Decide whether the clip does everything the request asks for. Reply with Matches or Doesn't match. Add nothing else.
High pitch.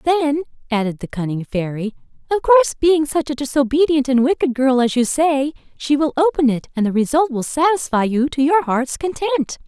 Matches